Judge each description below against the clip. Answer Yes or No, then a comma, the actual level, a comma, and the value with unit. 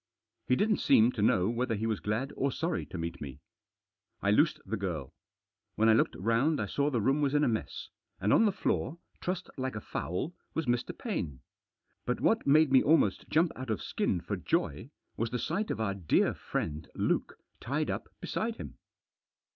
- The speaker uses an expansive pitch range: Yes, wide, 6.6 semitones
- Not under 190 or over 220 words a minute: Yes, average, 195 wpm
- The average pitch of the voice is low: Yes, low, 120 Hz